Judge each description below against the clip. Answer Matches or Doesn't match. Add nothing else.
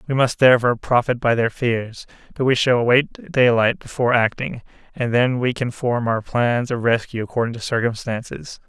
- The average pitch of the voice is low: Matches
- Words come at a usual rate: Matches